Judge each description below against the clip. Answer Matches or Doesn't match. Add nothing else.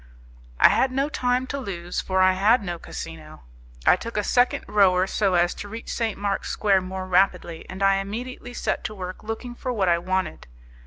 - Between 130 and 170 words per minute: Doesn't match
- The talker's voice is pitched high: Matches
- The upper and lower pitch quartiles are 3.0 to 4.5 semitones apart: Matches